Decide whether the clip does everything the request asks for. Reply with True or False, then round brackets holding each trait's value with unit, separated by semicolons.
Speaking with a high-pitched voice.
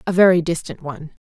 False (165 Hz)